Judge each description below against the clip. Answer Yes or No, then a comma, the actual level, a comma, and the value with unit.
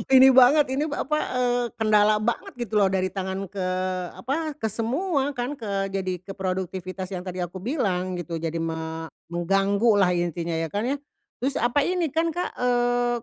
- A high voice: Yes, high, 205 Hz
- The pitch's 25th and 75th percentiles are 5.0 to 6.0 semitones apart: Yes, wide, 5.6 semitones